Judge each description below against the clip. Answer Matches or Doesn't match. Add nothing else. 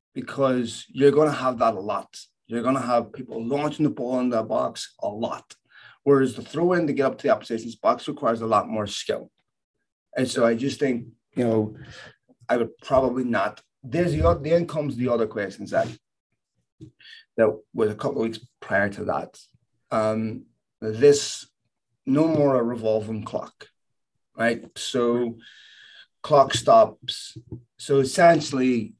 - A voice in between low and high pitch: Doesn't match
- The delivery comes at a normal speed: Matches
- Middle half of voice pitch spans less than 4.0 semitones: Matches